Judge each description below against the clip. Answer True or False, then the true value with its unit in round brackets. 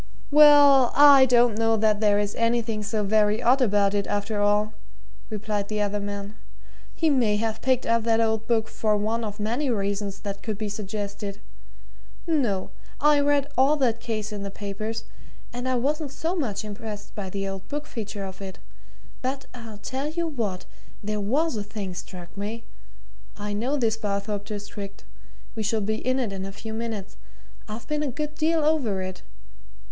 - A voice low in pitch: False (220 Hz)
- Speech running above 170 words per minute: True (180 wpm)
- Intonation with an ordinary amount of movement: True (3.6 semitones)